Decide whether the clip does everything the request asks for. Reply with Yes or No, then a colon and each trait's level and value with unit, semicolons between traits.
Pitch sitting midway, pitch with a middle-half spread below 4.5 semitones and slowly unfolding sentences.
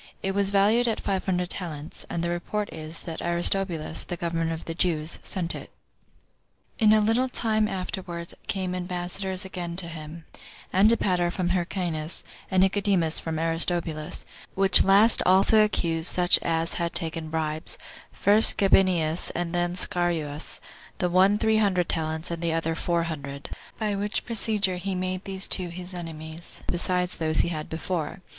No: medium, 175 Hz; average, 2.8 semitones; average, 160 wpm